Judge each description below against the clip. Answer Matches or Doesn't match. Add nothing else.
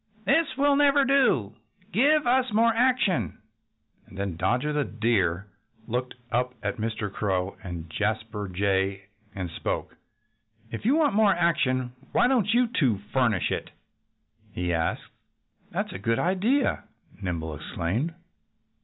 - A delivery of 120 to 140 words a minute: Matches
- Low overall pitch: Matches